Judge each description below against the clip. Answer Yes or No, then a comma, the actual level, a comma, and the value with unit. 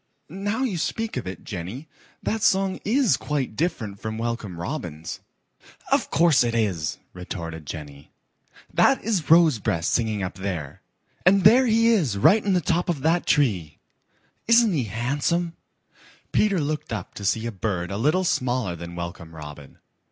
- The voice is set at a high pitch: No, low, 120 Hz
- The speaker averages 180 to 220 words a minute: No, average, 160 wpm